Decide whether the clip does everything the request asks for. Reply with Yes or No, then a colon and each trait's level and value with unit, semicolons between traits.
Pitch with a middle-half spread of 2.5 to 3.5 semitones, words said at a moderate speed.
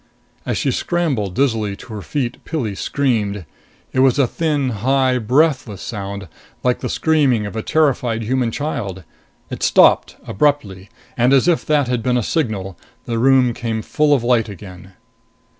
No: average, 4.8 semitones; average, 160 wpm